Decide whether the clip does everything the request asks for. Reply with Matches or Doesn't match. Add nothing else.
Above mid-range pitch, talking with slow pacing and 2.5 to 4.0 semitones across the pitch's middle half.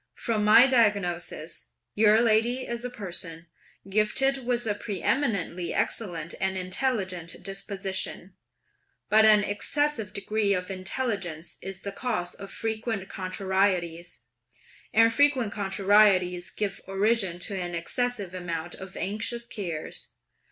Matches